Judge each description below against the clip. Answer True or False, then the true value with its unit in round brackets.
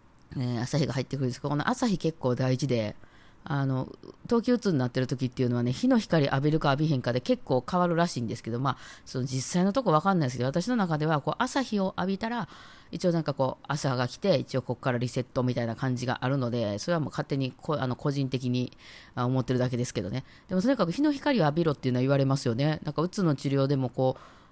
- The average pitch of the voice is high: False (140 Hz)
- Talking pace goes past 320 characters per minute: True (485 characters per minute)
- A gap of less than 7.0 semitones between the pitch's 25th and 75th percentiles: True (5.1 semitones)